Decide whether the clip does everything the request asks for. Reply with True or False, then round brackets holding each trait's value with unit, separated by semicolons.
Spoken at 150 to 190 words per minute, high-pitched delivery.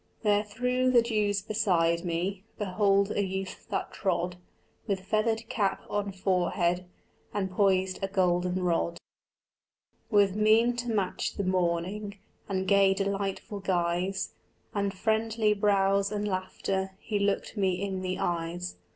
False (135 wpm; 195 Hz)